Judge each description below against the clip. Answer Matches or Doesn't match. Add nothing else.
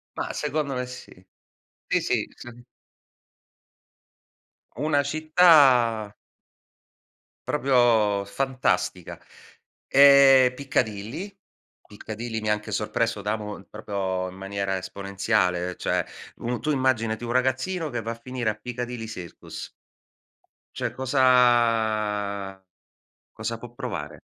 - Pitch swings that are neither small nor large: Matches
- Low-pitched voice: Matches